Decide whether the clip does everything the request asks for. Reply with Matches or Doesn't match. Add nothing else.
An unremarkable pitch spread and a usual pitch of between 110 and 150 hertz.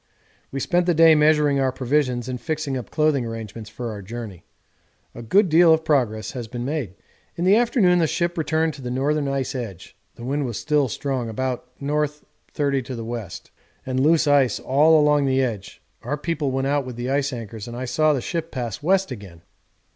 Matches